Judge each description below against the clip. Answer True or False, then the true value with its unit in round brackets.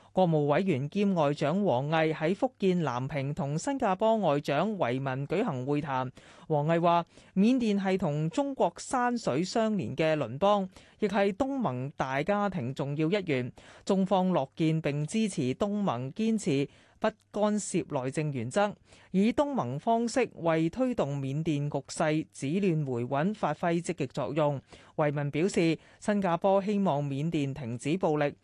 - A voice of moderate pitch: True (165 Hz)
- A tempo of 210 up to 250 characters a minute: True (230 characters per minute)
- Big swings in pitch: True (5.9 semitones)